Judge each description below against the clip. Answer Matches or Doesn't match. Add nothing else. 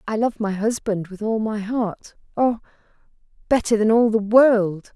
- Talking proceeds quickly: Doesn't match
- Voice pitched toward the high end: Matches